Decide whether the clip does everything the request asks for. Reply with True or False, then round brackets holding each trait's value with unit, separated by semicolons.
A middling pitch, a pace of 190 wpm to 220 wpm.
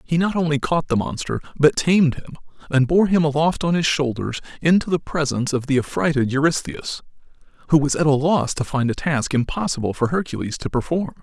True (150 Hz; 200 wpm)